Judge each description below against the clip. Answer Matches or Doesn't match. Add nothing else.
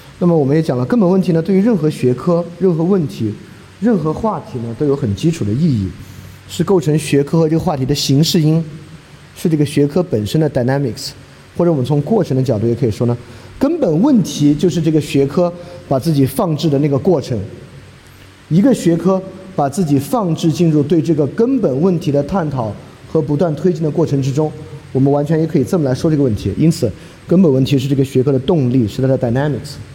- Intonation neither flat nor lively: Matches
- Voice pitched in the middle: Matches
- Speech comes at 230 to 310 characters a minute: Doesn't match